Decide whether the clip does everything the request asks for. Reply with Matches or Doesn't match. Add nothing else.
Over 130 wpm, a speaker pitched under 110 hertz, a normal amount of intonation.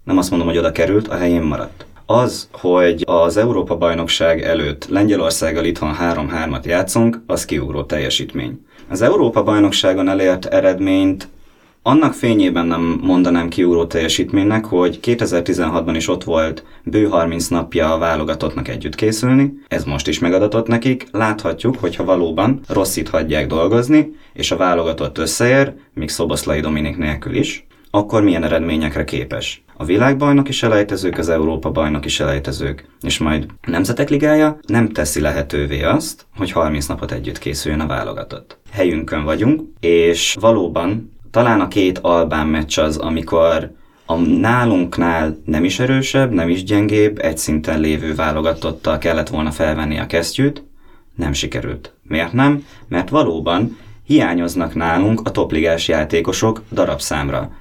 Doesn't match